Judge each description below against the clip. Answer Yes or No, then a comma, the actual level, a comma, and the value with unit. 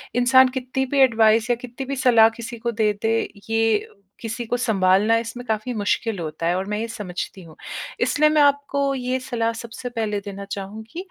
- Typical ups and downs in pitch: Yes, average, 3.0 semitones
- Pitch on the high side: Yes, high, 230 Hz